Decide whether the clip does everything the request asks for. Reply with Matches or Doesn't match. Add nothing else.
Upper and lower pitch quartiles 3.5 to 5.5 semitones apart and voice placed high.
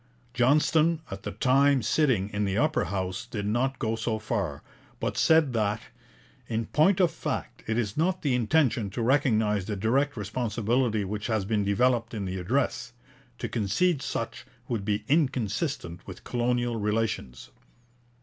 Doesn't match